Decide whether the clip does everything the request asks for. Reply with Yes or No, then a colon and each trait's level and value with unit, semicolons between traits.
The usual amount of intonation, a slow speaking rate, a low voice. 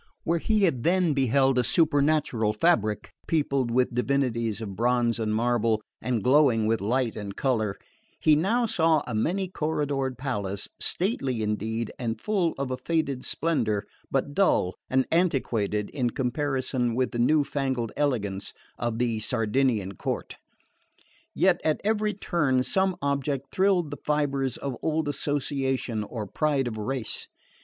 No: average, 4.8 semitones; average, 145 wpm; low, 130 Hz